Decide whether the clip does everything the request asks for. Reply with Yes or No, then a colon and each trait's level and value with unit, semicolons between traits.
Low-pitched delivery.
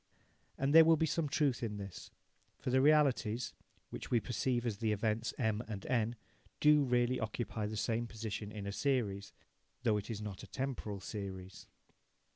Yes: low, 115 Hz